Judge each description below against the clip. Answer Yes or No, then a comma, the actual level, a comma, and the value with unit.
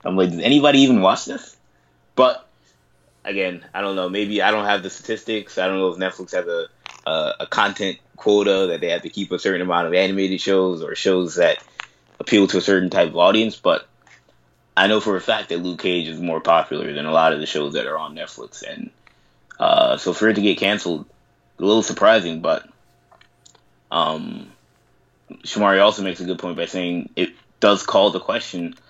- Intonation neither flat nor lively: Yes, average, 3.7 semitones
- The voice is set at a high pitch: No, very low, 95 Hz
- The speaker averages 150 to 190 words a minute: No, fast, 205 wpm